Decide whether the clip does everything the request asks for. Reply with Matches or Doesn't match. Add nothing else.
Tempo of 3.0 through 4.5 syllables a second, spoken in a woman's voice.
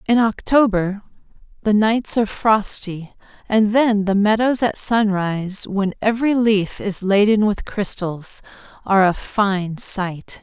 Matches